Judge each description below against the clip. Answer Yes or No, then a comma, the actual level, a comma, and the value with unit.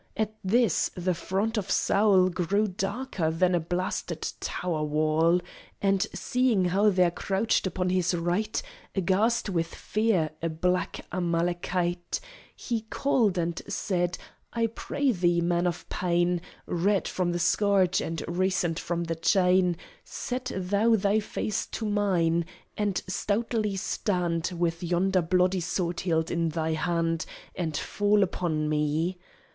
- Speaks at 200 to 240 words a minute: No, slow, 135 wpm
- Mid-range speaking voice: Yes, medium, 180 Hz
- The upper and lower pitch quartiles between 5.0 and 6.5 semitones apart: No, average, 3.0 semitones